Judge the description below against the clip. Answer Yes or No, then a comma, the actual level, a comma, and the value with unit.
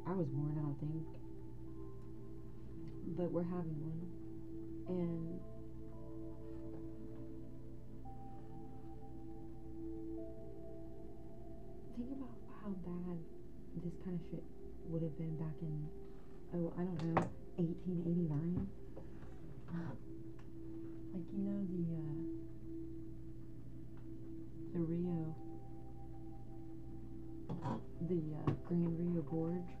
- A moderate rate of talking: No, slow, 85 wpm